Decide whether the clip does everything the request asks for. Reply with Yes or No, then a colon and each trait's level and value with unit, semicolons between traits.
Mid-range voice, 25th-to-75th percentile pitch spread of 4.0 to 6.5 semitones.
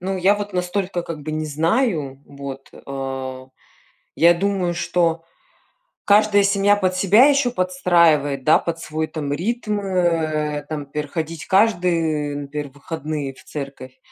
Yes: medium, 165 Hz; average, 4.5 semitones